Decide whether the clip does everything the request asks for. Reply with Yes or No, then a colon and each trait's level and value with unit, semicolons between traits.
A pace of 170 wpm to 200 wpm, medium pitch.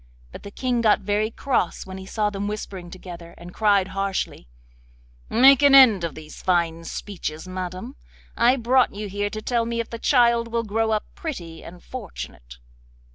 No: average, 180 wpm; high, 205 Hz